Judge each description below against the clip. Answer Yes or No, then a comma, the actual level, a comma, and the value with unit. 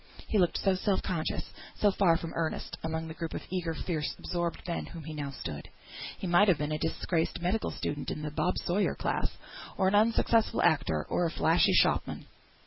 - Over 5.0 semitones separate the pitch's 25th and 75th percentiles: No, average, 2.9 semitones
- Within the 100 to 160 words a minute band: No, fast, 205 wpm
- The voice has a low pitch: No, medium, 170 Hz